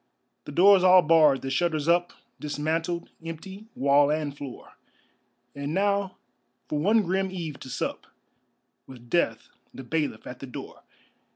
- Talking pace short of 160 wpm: Yes, average, 145 wpm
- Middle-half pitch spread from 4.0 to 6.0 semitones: Yes, average, 4.4 semitones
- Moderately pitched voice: Yes, medium, 160 Hz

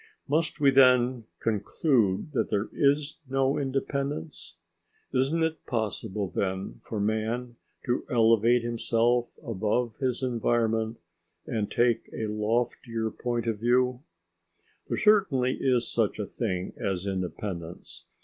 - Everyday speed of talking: No, slow, 120 wpm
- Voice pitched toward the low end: Yes, low, 120 Hz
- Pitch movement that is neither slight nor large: Yes, average, 3.2 semitones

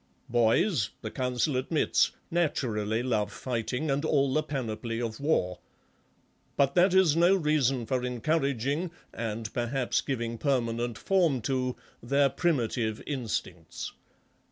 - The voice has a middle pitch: No, low, 125 Hz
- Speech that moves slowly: Yes, slow, 120 wpm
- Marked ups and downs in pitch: No, average, 4.4 semitones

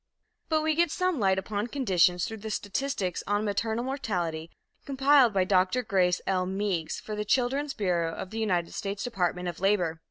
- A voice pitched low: No, high, 205 Hz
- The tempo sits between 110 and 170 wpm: No, average, 180 wpm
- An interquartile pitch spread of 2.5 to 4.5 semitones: No, average, 5.2 semitones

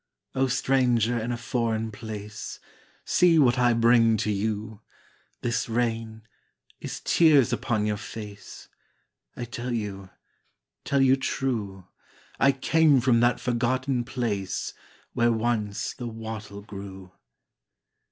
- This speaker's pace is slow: Yes, slow, 120 wpm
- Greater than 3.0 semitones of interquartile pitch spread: No, average, 2.7 semitones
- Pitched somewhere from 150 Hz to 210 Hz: No, low, 115 Hz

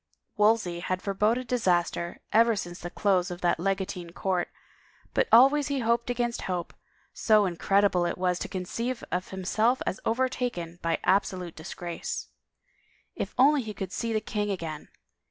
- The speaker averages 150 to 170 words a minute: Yes, average, 155 wpm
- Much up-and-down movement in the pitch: No, average, 4.6 semitones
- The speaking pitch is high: Yes, high, 195 Hz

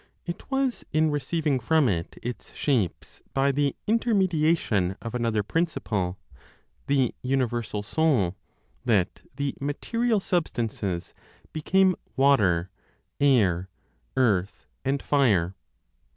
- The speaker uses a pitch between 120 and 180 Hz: Yes, low, 135 Hz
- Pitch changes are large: Yes, wide, 7.3 semitones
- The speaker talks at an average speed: No, slow, 100 wpm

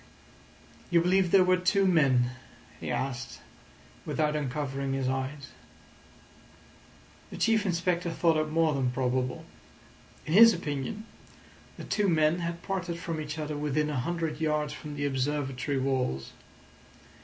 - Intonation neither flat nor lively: Yes, average, 4.0 semitones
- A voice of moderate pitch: Yes, medium, 150 Hz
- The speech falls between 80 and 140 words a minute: Yes, slow, 135 wpm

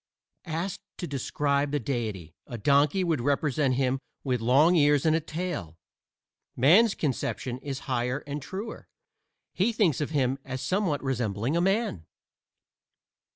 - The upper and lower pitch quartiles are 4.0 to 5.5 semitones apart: Yes, average, 4.4 semitones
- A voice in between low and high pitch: Yes, medium, 145 Hz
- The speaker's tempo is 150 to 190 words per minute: No, average, 140 wpm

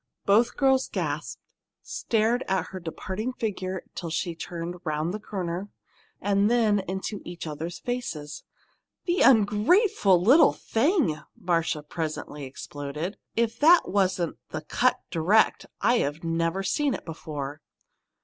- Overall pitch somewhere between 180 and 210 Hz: Yes, high, 190 Hz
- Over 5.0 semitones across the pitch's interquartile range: Yes, wide, 5.6 semitones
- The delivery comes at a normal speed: No, slow, 120 wpm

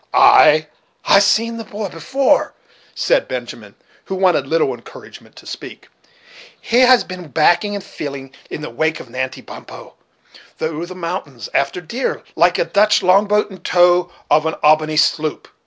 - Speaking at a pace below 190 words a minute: Yes, average, 165 wpm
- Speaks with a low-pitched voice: No, medium, 175 Hz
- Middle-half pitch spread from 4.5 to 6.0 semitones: Yes, average, 5.0 semitones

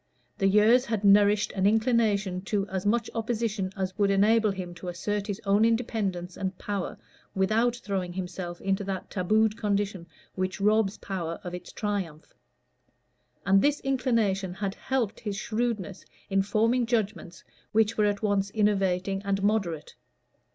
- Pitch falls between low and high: No, high, 200 Hz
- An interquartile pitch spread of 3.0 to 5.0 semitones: No, narrow, 2.4 semitones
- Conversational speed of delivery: Yes, average, 150 wpm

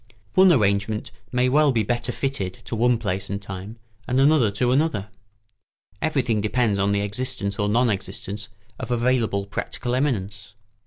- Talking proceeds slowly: No, average, 155 wpm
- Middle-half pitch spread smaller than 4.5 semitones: Yes, average, 4.0 semitones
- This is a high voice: No, low, 115 Hz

